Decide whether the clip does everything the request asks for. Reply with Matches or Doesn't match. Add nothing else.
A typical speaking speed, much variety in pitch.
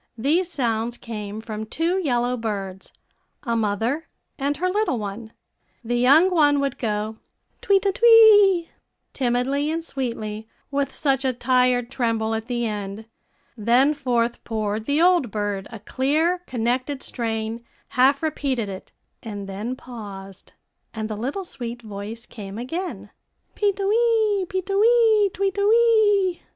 Matches